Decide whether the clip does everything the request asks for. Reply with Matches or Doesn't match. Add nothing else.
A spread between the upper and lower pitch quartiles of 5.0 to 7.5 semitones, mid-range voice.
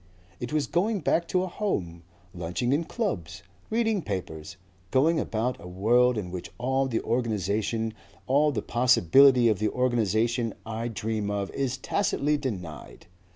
Doesn't match